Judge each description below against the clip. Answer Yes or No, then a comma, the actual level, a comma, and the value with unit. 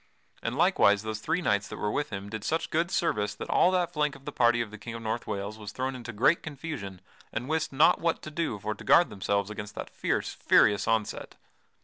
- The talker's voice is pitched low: Yes, low, 115 Hz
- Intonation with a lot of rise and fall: Yes, wide, 6.8 semitones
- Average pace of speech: No, fast, 235 wpm